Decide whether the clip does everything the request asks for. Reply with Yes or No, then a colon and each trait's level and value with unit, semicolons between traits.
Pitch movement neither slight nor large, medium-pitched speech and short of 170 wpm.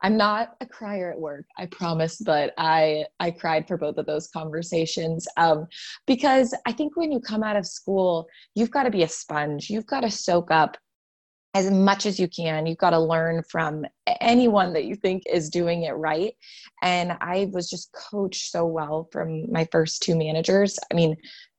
No: average, 4.2 semitones; medium, 175 Hz; average, 195 wpm